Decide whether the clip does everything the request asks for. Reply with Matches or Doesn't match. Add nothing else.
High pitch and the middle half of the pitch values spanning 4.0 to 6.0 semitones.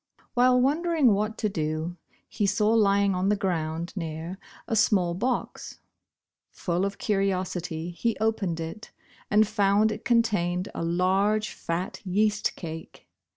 Doesn't match